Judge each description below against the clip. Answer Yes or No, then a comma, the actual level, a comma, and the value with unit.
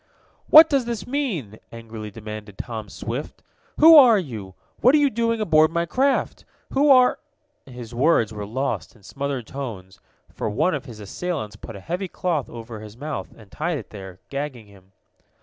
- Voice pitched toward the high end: No, low, 135 Hz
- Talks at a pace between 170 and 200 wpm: Yes, average, 180 wpm